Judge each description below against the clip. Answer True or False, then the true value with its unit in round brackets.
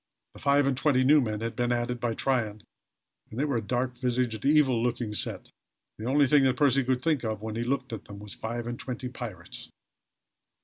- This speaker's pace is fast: True (220 wpm)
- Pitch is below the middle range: True (125 Hz)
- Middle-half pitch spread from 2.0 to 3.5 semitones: True (2.8 semitones)